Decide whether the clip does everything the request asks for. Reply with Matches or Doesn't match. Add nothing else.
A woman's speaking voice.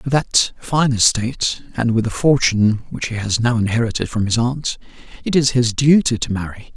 Doesn't match